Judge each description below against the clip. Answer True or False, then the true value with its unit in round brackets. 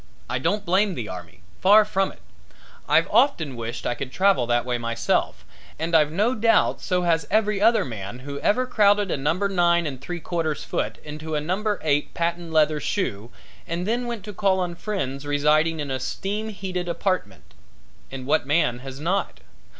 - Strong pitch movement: True (6.3 semitones)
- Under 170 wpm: False (185 wpm)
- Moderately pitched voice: True (165 Hz)